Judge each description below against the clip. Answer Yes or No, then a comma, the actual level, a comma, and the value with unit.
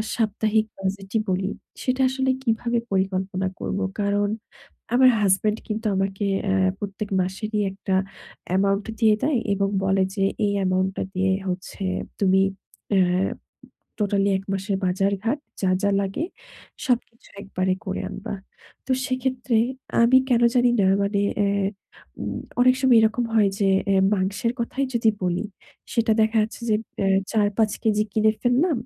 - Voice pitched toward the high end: Yes, high, 205 Hz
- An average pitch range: Yes, average, 3.1 semitones